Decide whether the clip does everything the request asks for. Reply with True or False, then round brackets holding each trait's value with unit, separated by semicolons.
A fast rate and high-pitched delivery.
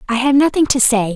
True (260 wpm; 250 Hz)